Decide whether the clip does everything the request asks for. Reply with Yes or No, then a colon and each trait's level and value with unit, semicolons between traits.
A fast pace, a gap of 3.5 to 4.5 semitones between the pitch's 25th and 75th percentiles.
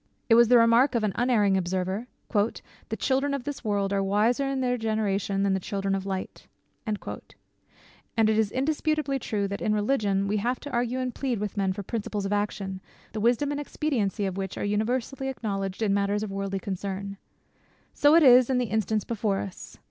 No: average, 195 wpm; average, 4.0 semitones